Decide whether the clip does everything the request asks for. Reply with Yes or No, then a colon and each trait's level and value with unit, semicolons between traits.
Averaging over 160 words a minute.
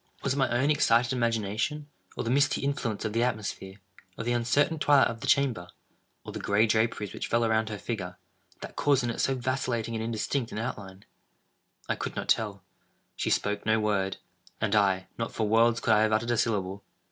Yes: average, 185 wpm